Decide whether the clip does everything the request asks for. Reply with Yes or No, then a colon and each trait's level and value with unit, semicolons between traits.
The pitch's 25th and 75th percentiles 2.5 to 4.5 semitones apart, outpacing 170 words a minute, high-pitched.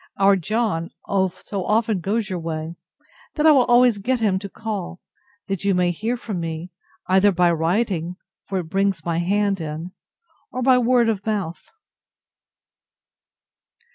No: average, 4.1 semitones; average, 150 wpm; high, 195 Hz